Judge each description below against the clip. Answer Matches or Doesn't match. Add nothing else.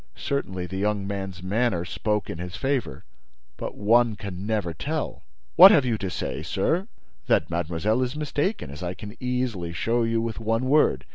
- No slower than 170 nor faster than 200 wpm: Matches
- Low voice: Matches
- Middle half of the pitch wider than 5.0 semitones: Matches